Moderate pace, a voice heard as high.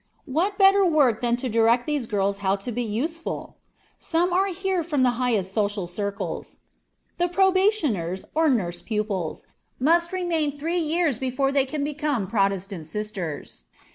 Yes: average, 150 wpm; very high, 255 Hz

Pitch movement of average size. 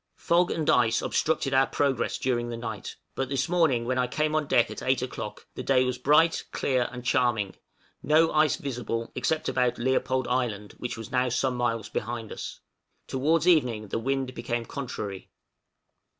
Yes: average, 3.0 semitones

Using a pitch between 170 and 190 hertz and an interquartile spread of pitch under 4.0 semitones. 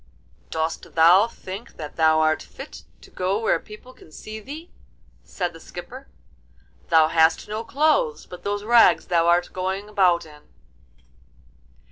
No: medium, 185 Hz; average, 4.9 semitones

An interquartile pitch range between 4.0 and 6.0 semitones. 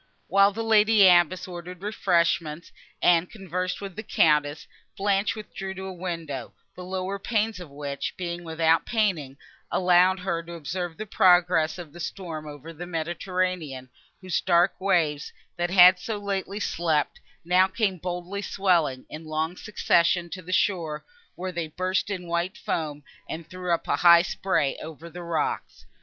No: narrow, 2.6 semitones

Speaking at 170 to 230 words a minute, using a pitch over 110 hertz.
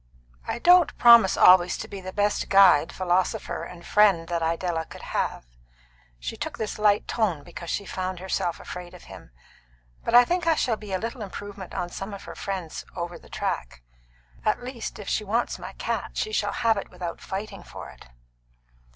Yes: average, 190 wpm; high, 190 Hz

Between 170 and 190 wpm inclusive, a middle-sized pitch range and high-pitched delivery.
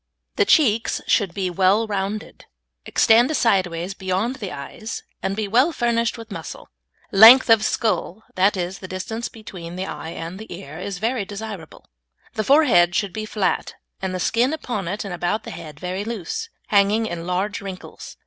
Yes: average, 175 wpm; average, 3.5 semitones; high, 200 Hz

